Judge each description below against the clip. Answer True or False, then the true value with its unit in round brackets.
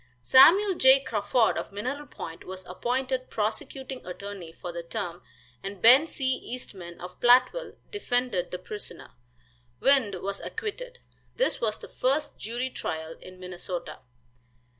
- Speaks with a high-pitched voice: True (225 Hz)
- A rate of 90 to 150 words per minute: True (135 wpm)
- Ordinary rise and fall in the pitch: False (6.2 semitones)